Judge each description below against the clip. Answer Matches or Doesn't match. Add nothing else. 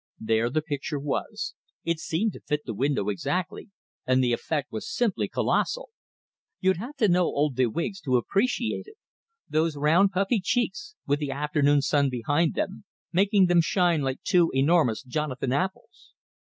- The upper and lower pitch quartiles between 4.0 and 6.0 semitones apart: Matches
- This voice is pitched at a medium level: Matches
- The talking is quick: Doesn't match